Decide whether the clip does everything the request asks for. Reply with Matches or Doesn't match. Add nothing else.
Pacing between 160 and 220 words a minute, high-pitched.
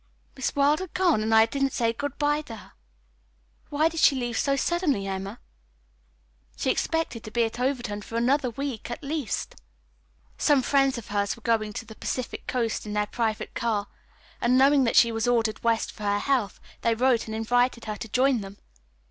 Matches